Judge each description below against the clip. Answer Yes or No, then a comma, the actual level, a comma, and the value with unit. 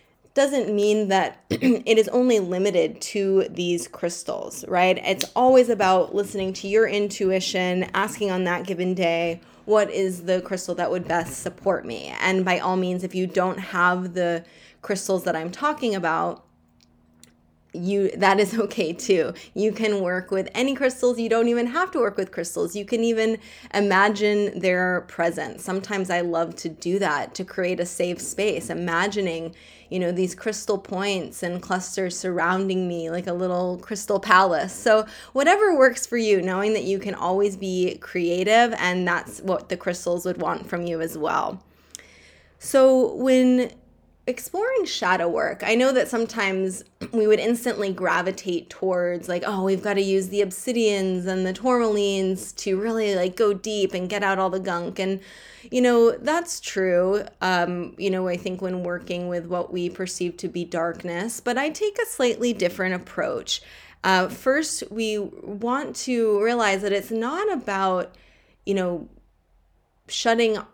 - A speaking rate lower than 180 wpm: Yes, average, 165 wpm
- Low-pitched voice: No, high, 190 Hz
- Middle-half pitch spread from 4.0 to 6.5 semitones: No, average, 3.5 semitones